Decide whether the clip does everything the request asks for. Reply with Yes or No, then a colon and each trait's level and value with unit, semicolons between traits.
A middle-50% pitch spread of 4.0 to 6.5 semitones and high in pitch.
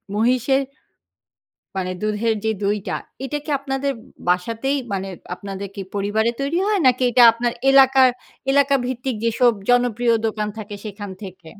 Yes: average, 4.4 semitones; high, 230 Hz